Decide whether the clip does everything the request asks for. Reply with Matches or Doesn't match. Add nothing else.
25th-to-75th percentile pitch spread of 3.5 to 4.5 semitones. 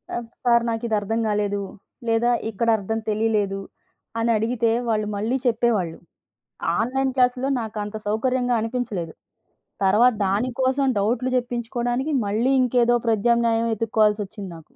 Doesn't match